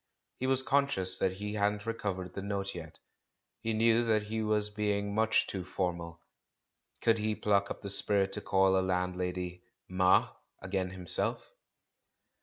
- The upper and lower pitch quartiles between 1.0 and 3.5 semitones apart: Yes, narrow, 2.6 semitones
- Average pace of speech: Yes, average, 160 wpm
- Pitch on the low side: Yes, low, 100 Hz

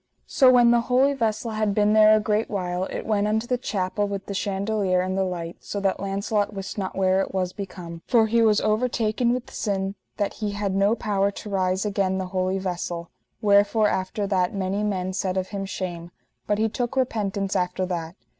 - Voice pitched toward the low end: No, high, 200 Hz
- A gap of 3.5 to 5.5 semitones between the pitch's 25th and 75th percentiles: No, narrow, 2.4 semitones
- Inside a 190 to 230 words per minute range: Yes, fast, 205 wpm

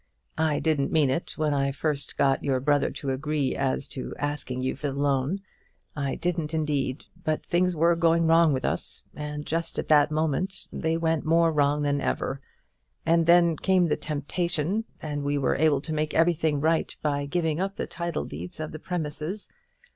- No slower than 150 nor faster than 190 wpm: Yes, average, 185 wpm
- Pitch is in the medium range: Yes, medium, 150 Hz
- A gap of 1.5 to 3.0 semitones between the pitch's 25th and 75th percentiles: Yes, average, 2.7 semitones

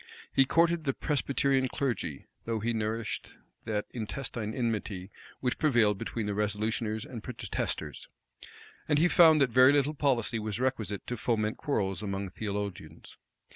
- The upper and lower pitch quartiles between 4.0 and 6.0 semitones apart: Yes, average, 4.3 semitones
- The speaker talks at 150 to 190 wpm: No, average, 140 wpm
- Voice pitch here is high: No, low, 115 Hz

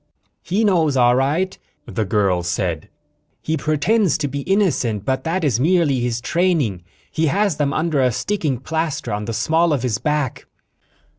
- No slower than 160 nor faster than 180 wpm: Yes, average, 165 wpm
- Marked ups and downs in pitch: Yes, wide, 5.8 semitones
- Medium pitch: Yes, medium, 145 Hz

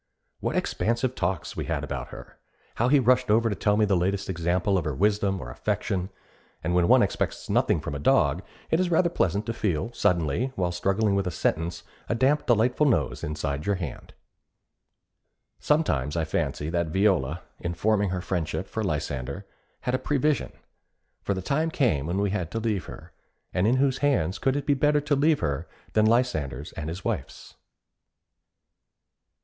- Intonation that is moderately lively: No, wide, 6.6 semitones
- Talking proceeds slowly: No, average, 180 wpm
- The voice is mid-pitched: No, low, 100 Hz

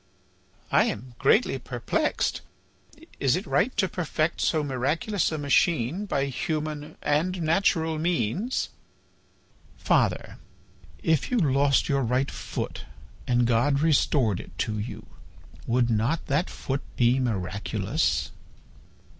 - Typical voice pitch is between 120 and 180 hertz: Yes, medium, 140 Hz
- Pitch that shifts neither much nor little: Yes, average, 4.8 semitones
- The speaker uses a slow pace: Yes, slow, 115 wpm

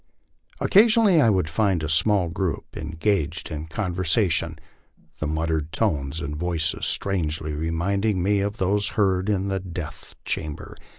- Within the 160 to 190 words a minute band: No, average, 140 wpm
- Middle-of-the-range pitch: No, very low, 90 Hz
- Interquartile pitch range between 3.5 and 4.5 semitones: Yes, average, 4.1 semitones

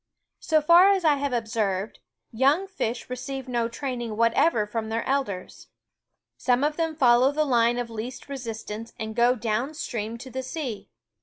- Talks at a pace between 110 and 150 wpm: No, average, 180 wpm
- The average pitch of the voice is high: Yes, high, 245 Hz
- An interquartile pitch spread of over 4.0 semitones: No, average, 3.6 semitones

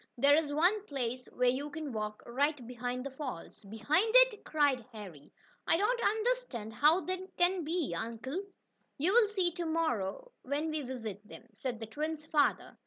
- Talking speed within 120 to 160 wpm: No, average, 170 wpm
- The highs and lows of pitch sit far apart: Yes, wide, 6.5 semitones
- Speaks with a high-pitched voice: Yes, very high, 290 Hz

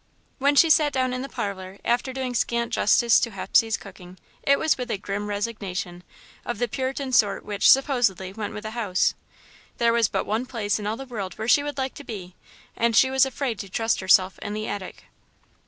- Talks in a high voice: Yes, high, 230 Hz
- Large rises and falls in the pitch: No, average, 4.4 semitones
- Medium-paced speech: No, fast, 210 wpm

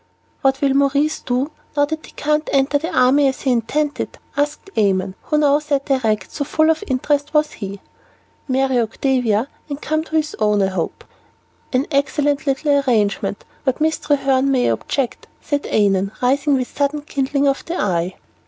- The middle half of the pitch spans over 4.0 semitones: No, average, 3.0 semitones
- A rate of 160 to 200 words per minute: Yes, average, 170 wpm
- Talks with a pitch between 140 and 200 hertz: No, very high, 275 Hz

